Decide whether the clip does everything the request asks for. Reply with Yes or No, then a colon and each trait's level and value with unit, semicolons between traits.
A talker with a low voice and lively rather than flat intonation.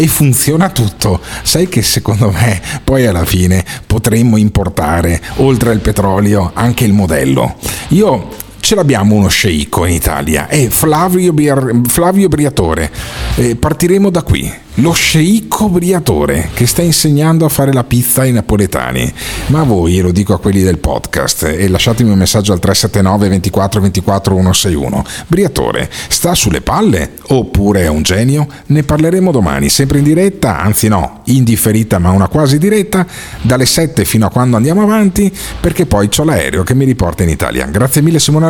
Yes: low, 115 Hz; wide, 7.6 semitones